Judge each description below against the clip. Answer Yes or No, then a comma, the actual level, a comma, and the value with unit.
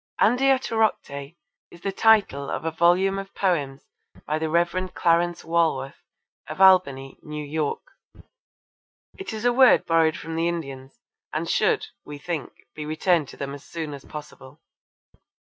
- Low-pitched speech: No, medium, 165 Hz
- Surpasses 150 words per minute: No, average, 145 wpm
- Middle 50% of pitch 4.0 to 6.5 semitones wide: Yes, average, 4.5 semitones